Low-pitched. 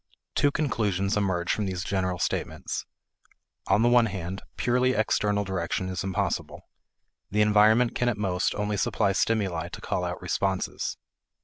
Yes: low, 100 Hz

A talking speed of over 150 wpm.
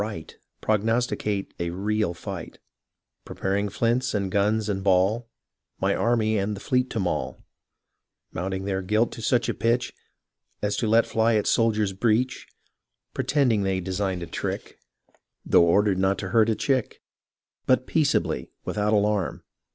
No: average, 145 wpm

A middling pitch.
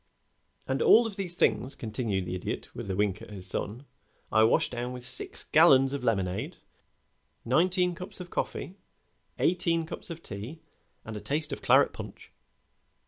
No: low, 125 Hz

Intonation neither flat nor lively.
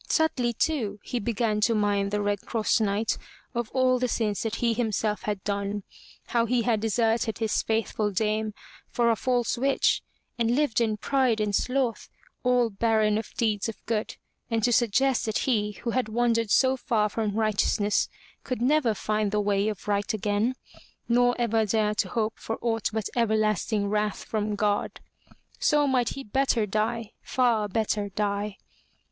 No: narrow, 2.3 semitones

